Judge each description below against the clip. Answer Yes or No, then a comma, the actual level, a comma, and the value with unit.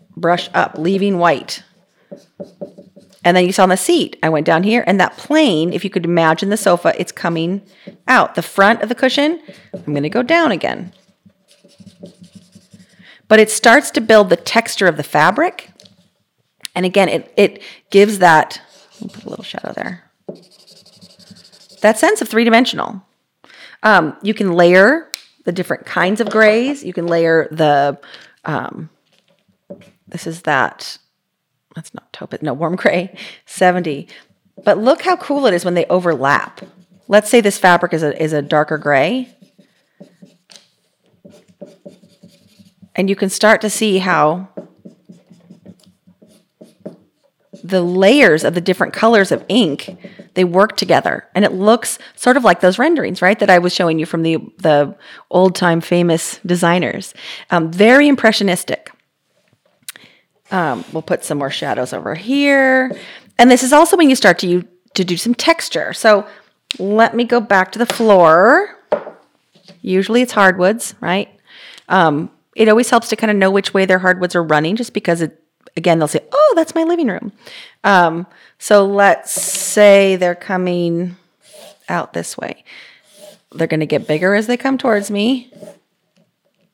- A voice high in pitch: Yes, high, 195 Hz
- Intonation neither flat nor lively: Yes, average, 3.6 semitones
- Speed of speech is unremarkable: Yes, average, 155 wpm